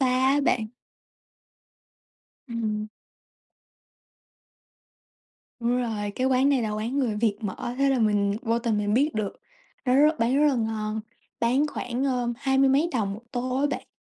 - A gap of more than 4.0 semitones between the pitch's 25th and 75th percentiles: No, average, 3.6 semitones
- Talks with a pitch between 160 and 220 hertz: No, high, 240 Hz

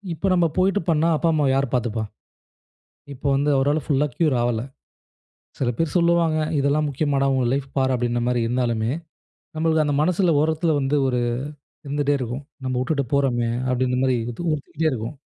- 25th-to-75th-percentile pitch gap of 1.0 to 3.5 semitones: No, average, 3.9 semitones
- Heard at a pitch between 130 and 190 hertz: Yes, medium, 140 Hz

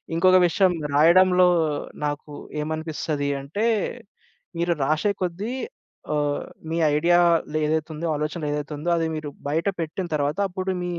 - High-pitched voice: No, medium, 160 Hz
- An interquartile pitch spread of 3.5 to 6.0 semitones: No, average, 2.9 semitones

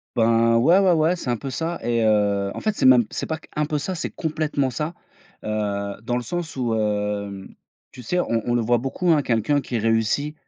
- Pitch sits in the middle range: No, low, 120 Hz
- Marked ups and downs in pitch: Yes, wide, 5.8 semitones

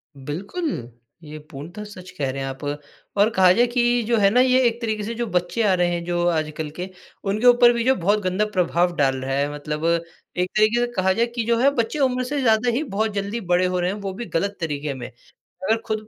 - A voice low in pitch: No, high, 195 Hz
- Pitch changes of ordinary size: No, wide, 5.7 semitones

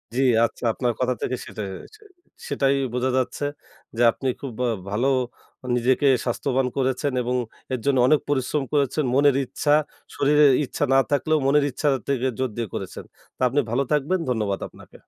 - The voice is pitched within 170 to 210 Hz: No, low, 130 Hz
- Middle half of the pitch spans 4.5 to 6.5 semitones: No, narrow, 2.4 semitones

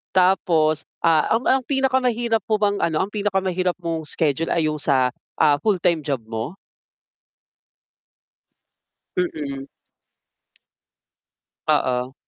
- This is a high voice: No, medium, 170 Hz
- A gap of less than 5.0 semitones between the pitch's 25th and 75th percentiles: No, wide, 5.4 semitones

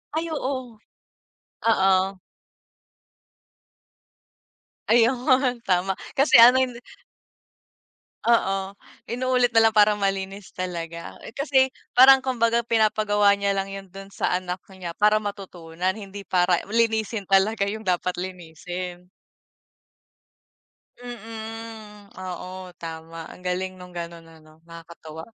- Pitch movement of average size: Yes, average, 3.9 semitones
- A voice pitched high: Yes, high, 195 Hz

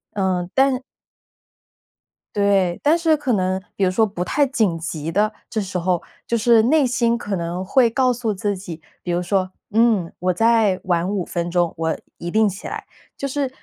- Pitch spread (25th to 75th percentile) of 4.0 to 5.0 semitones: Yes, average, 4.7 semitones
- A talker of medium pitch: No, high, 200 Hz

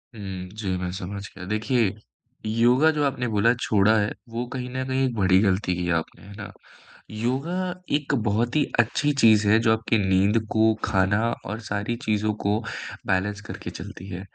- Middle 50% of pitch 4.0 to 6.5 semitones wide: No, average, 2.9 semitones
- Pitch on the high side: No, low, 110 Hz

